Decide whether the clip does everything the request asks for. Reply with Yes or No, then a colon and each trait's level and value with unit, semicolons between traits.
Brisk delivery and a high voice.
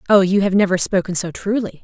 Yes: fast, 230 wpm; high, 195 Hz